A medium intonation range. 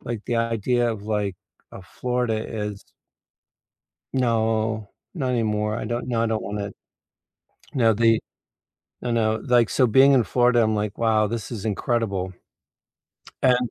No: narrow, 2.2 semitones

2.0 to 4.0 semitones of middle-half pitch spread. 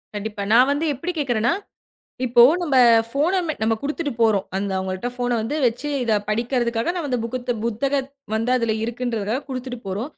Yes: average, 3.6 semitones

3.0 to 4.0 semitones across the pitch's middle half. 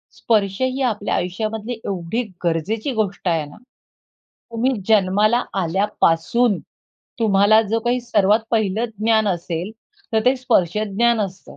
Yes: average, 3.5 semitones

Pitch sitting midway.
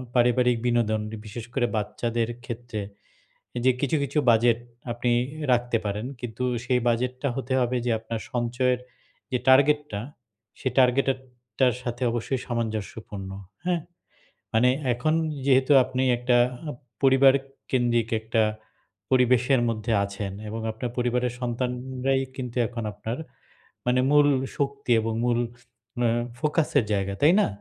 No: low, 125 Hz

